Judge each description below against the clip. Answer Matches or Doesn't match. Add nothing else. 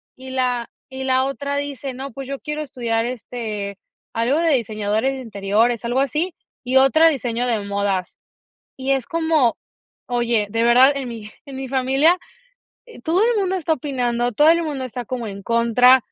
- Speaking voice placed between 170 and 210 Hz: Doesn't match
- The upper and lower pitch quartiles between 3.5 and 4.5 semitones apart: Doesn't match